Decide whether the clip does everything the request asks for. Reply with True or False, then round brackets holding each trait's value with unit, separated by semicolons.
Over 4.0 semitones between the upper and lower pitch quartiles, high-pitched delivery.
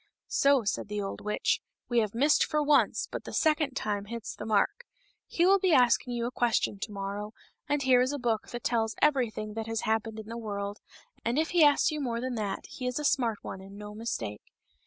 True (4.7 semitones; 235 Hz)